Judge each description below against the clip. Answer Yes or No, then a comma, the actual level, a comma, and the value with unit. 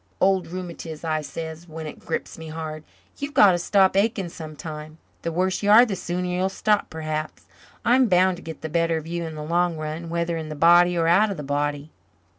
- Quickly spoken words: Yes, fast, 220 wpm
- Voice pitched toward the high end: No, medium, 170 Hz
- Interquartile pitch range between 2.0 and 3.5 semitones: Yes, average, 2.8 semitones